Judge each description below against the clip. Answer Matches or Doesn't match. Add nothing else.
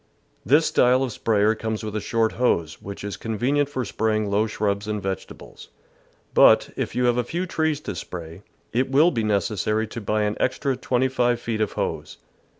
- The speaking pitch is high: Doesn't match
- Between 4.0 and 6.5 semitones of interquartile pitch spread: Doesn't match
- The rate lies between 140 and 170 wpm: Doesn't match